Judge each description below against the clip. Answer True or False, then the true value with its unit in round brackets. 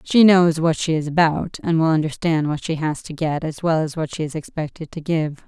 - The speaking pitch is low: False (160 Hz)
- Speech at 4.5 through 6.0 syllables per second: True (5.3 syllables/s)